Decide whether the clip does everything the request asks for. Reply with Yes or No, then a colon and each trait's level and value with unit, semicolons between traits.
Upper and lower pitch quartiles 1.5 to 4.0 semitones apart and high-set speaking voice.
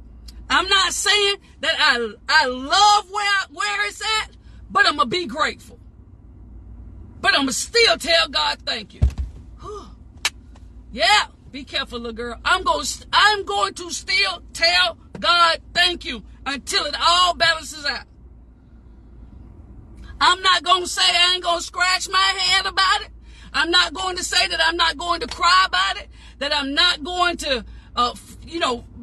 Yes: average, 3.1 semitones; very high, 355 Hz